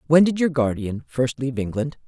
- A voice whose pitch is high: No, low, 135 Hz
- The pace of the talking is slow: No, fast, 205 wpm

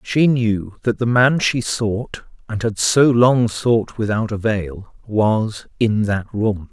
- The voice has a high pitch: No, low, 110 Hz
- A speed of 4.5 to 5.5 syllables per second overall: No, 3.3 syllables/s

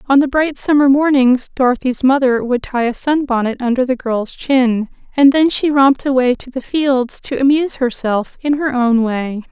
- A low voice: No, very high, 260 Hz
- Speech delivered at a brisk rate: No, average, 195 wpm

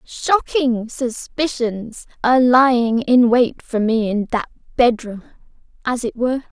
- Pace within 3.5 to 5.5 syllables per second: Yes, 4.0 syllables/s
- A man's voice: No, female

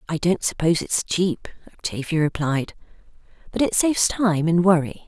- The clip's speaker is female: Yes, female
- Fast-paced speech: No, average, 155 wpm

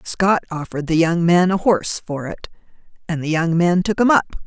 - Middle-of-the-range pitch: Yes, medium, 175 Hz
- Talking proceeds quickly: Yes, fast, 215 wpm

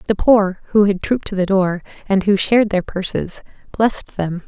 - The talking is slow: No, average, 200 wpm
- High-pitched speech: Yes, high, 195 Hz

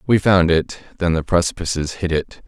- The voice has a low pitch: Yes, very low, 85 Hz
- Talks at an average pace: Yes, average, 195 wpm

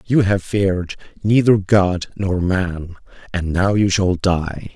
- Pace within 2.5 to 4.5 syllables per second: Yes, 3.6 syllables/s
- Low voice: Yes, very low, 95 Hz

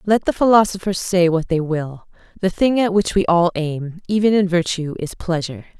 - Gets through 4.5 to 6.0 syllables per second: Yes, 5.2 syllables/s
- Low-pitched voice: No, medium, 180 Hz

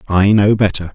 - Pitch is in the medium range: No, low, 100 Hz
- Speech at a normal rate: Yes, average, 190 wpm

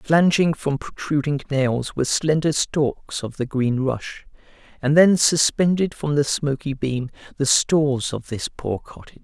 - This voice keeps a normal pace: Yes, average, 155 wpm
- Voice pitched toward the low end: No, medium, 145 Hz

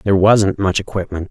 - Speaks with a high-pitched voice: No, very low, 95 Hz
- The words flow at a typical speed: Yes, average, 185 wpm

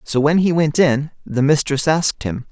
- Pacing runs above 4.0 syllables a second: Yes, 4.8 syllables/s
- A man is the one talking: Yes, male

